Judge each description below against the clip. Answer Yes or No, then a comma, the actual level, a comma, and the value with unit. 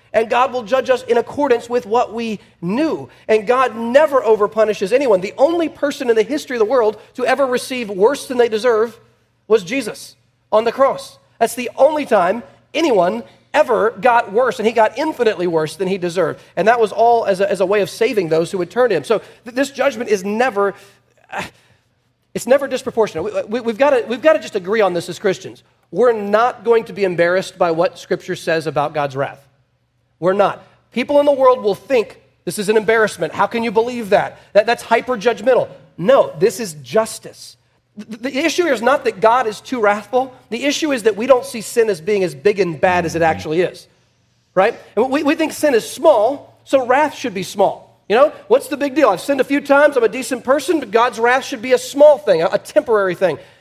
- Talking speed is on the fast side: Yes, fast, 220 wpm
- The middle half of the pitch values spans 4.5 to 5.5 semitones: Yes, average, 5.2 semitones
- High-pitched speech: Yes, high, 230 Hz